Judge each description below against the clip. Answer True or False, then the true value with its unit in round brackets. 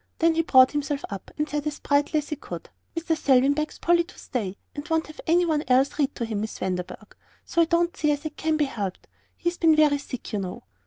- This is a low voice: False (295 Hz)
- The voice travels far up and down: False (3.8 semitones)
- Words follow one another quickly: True (245 wpm)